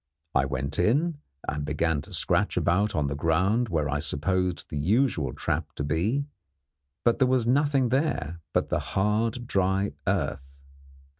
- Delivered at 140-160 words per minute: Yes, average, 155 wpm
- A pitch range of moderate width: No, wide, 7.8 semitones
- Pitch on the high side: No, very low, 90 Hz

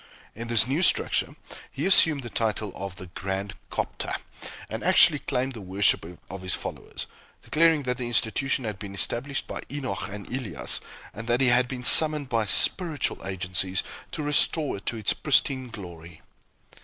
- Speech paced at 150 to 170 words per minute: Yes, average, 165 wpm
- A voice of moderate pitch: No, low, 115 Hz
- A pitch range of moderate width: No, wide, 5.7 semitones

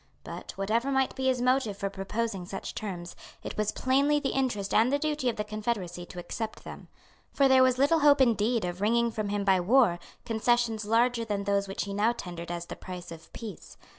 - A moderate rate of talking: No, fast, 210 wpm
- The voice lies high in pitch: Yes, high, 220 Hz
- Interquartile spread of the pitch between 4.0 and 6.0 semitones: Yes, average, 4.4 semitones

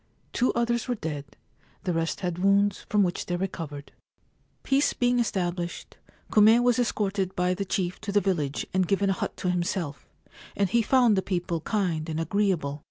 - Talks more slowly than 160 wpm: No, average, 175 wpm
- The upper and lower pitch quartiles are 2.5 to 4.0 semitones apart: Yes, average, 3.4 semitones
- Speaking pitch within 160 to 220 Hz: Yes, high, 190 Hz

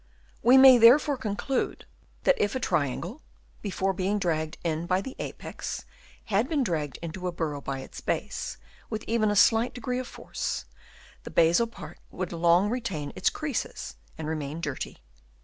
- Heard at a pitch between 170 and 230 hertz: Yes, high, 190 Hz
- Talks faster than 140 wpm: Yes, average, 165 wpm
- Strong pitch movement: Yes, wide, 6.5 semitones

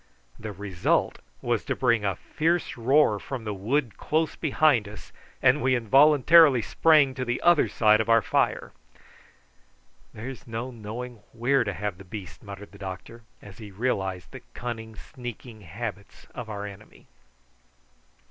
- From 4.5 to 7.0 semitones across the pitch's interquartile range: No, average, 4.0 semitones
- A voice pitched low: Yes, low, 115 Hz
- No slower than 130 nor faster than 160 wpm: Yes, average, 150 wpm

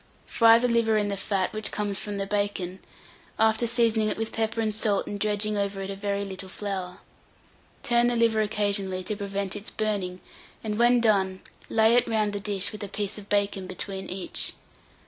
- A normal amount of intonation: No, narrow, 1.9 semitones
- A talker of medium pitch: No, high, 205 Hz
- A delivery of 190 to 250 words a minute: Yes, average, 195 wpm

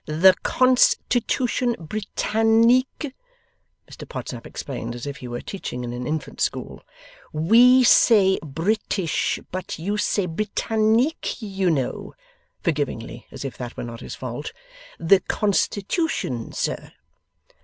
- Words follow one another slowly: Yes, slow, 120 wpm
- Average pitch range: No, wide, 8.3 semitones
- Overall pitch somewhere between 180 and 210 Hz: Yes, high, 190 Hz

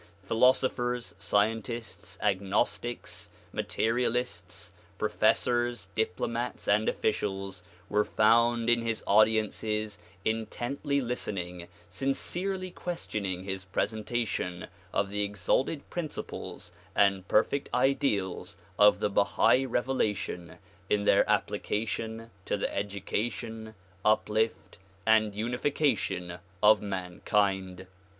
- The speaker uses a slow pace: Yes, slow, 90 wpm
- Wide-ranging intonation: No, average, 3.3 semitones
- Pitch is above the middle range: No, low, 110 Hz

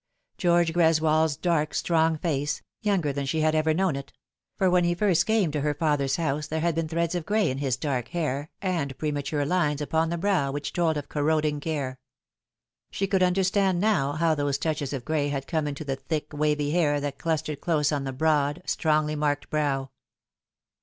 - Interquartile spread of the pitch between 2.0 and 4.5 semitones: Yes, average, 2.7 semitones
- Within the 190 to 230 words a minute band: Yes, average, 195 wpm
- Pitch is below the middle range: No, medium, 155 Hz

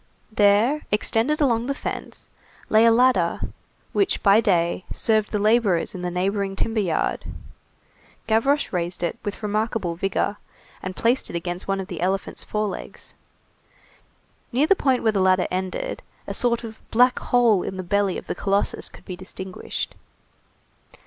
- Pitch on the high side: Yes, high, 205 Hz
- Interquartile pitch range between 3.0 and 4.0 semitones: Yes, average, 3.7 semitones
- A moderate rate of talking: Yes, average, 155 wpm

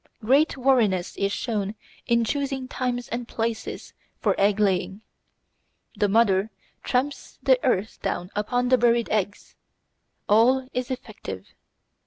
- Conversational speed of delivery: No, slow, 125 wpm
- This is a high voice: Yes, high, 230 Hz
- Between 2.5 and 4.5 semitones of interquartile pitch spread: Yes, average, 3.7 semitones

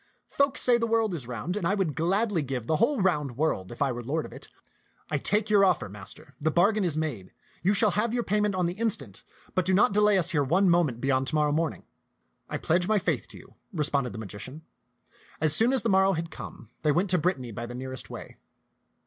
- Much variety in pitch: Yes, wide, 6.6 semitones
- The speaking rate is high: Yes, fast, 235 wpm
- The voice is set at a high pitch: No, medium, 170 Hz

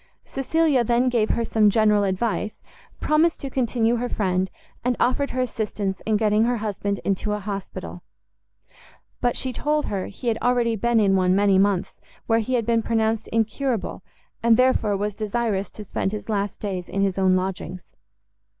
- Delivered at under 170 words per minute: No, average, 175 wpm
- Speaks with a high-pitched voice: Yes, high, 220 Hz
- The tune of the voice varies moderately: Yes, average, 3.2 semitones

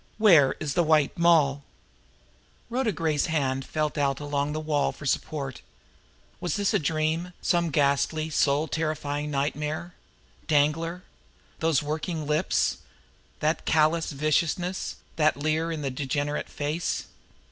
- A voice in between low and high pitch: Yes, medium, 155 Hz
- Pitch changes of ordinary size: No, narrow, 2.1 semitones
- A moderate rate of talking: No, slow, 125 wpm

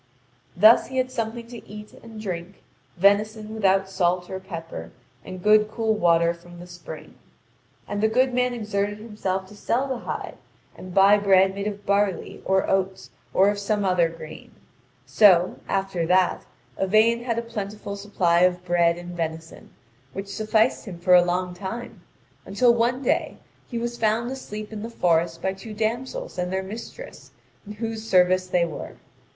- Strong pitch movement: No, average, 3.5 semitones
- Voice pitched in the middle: No, high, 200 Hz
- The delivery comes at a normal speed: Yes, average, 170 wpm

